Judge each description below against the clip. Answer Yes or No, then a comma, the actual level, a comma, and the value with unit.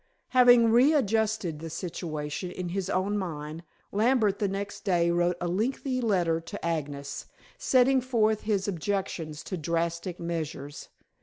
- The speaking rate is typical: No, slow, 130 wpm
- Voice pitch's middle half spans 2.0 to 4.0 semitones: No, average, 4.7 semitones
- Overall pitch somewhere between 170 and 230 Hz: Yes, medium, 185 Hz